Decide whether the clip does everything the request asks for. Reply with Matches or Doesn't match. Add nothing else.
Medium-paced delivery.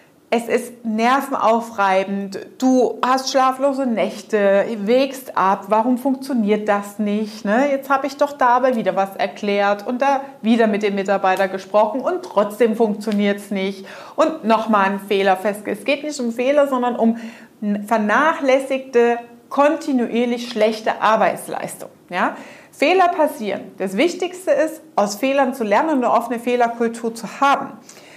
Matches